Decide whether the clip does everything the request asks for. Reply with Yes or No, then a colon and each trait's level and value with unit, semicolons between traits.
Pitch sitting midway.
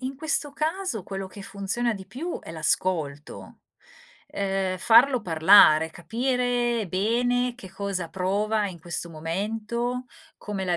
No: high, 200 Hz